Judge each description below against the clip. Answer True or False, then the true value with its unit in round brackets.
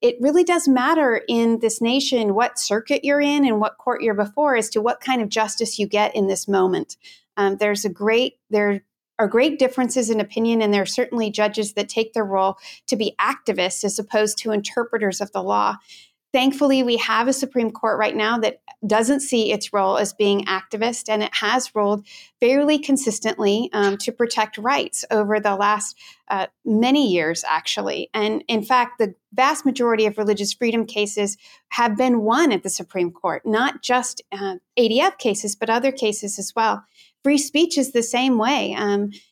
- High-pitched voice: True (225 Hz)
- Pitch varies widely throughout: False (3.4 semitones)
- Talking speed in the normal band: True (190 wpm)